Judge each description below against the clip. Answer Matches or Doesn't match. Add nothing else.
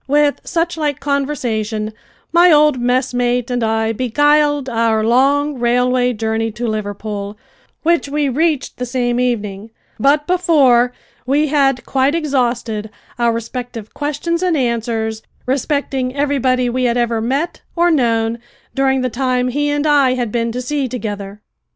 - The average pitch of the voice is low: Doesn't match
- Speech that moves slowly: Doesn't match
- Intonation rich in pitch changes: Doesn't match